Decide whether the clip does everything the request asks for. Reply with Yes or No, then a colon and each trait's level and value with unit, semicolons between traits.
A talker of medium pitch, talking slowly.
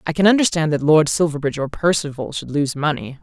No: medium, 155 Hz; fast, 205 wpm